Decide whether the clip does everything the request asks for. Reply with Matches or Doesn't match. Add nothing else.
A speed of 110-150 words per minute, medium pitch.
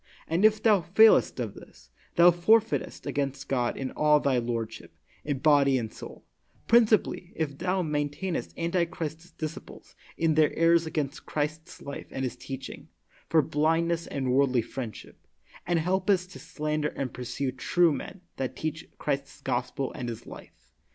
Doesn't match